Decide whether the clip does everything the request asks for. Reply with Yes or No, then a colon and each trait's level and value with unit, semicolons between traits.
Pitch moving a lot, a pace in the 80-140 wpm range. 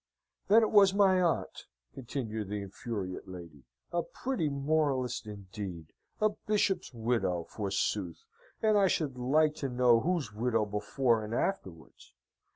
Yes: wide, 7.4 semitones; slow, 135 wpm